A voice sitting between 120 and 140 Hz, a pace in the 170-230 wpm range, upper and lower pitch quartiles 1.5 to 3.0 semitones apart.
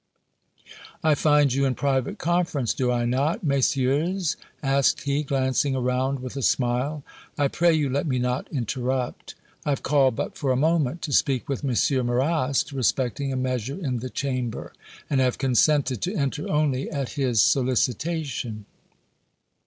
No: low, 135 Hz; average, 155 wpm; narrow, 2.4 semitones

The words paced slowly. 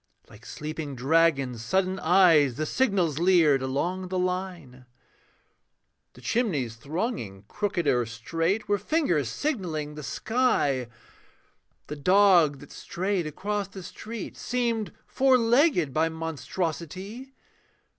Yes: slow, 115 wpm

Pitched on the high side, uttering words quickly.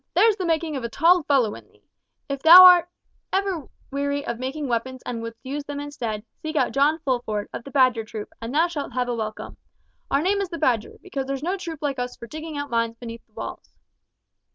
Yes: very high, 275 Hz; fast, 225 wpm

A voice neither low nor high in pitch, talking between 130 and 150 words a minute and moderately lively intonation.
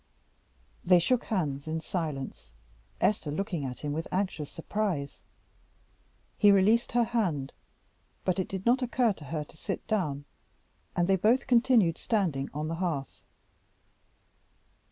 No: medium, 180 Hz; slow, 135 wpm; wide, 6.1 semitones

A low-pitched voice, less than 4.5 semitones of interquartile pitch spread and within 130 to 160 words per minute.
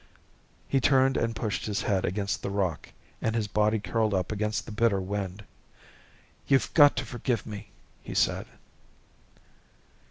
Yes: low, 105 Hz; narrow, 2.5 semitones; average, 150 wpm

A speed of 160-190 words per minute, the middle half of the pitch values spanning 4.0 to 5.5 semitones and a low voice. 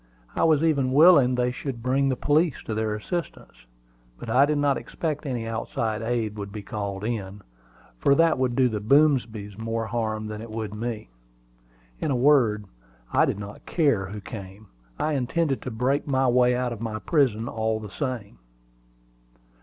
Yes: average, 175 wpm; average, 4.3 semitones; low, 120 Hz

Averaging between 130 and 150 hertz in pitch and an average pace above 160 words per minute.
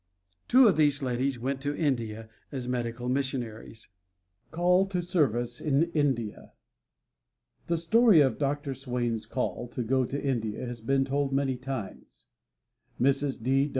No: low, 135 Hz; slow, 135 wpm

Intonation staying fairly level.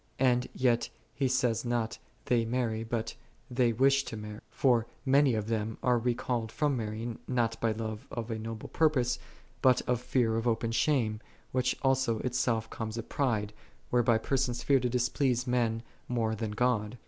Yes: narrow, 2.1 semitones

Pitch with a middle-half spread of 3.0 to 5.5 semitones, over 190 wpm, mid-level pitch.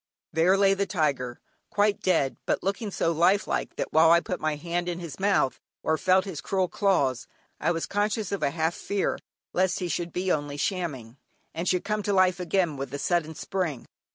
Yes: average, 3.6 semitones; average, 200 wpm; medium, 175 Hz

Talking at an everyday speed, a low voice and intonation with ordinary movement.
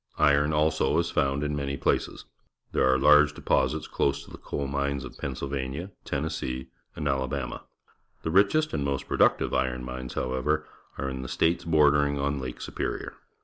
No: average, 165 wpm; very low, 70 Hz; narrow, 2.3 semitones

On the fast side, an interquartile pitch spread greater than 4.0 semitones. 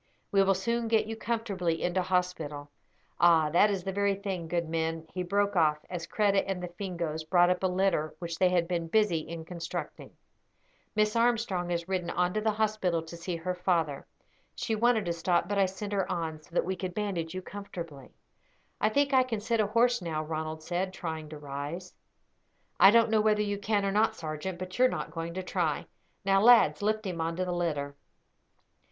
No: fast, 210 wpm; average, 3.5 semitones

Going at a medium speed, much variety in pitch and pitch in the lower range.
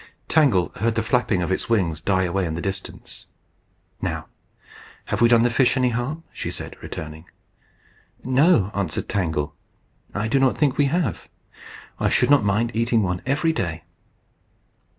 Yes: average, 160 wpm; wide, 5.9 semitones; low, 115 Hz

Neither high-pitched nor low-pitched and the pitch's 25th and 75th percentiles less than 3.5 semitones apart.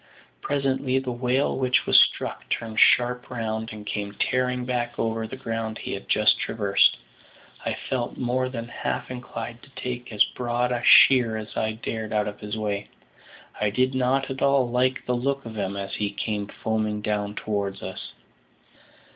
No: low, 120 Hz; average, 2.9 semitones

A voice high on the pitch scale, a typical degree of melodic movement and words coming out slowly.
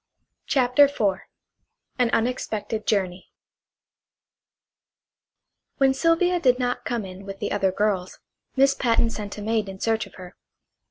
Yes: high, 225 Hz; average, 4.4 semitones; slow, 130 wpm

